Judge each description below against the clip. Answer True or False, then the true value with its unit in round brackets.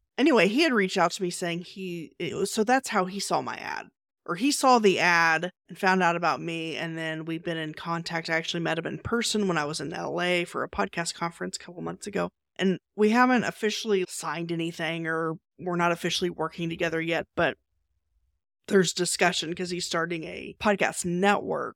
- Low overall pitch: False (170 Hz)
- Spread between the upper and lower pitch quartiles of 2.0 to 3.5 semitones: True (2.8 semitones)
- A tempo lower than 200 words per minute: False (205 wpm)